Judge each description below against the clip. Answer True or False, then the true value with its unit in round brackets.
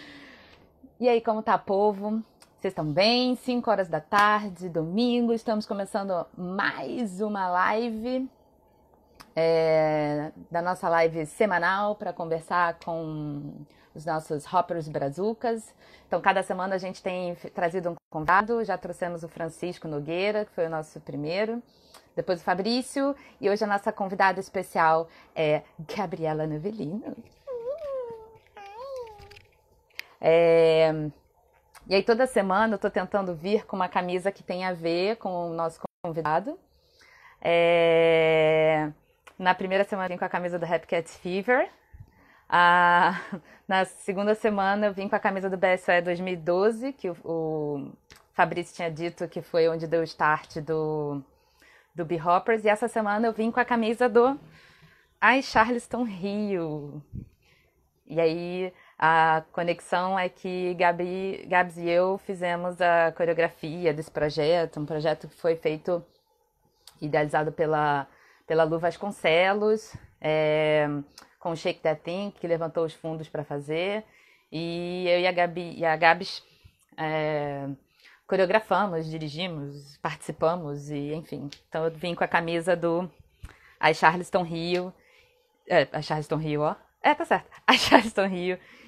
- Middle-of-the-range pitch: True (180 Hz)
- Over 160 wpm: False (140 wpm)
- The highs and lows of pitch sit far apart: False (4.0 semitones)